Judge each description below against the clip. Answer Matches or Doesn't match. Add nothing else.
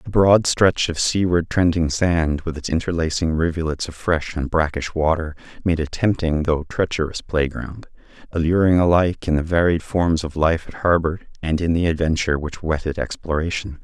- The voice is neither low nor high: Doesn't match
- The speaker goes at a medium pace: Matches